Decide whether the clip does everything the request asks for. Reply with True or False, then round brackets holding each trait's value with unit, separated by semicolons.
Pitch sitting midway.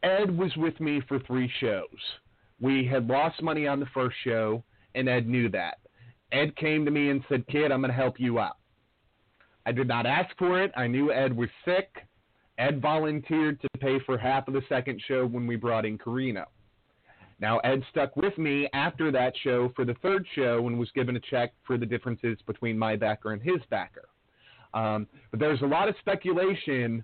False (130 Hz)